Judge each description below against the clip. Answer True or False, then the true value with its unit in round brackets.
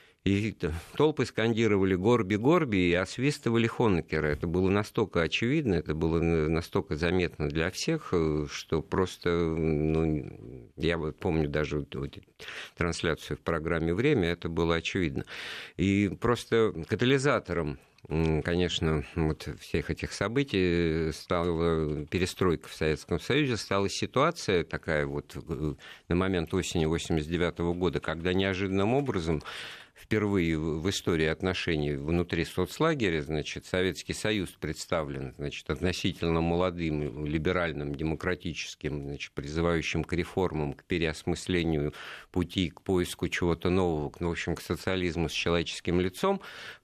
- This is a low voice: True (85 Hz)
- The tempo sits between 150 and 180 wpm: False (115 wpm)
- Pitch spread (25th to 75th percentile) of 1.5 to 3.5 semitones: True (3.1 semitones)